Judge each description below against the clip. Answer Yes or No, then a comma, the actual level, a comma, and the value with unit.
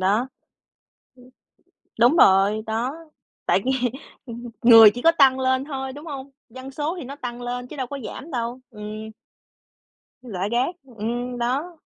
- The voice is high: Yes, high, 245 Hz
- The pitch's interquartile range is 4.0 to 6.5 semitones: No, average, 2.8 semitones